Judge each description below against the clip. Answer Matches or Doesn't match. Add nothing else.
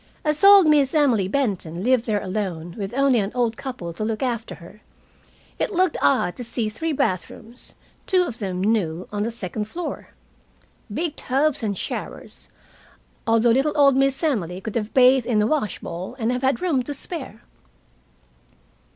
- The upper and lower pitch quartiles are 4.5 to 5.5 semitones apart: Matches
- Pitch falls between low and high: Doesn't match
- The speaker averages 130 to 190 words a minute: Matches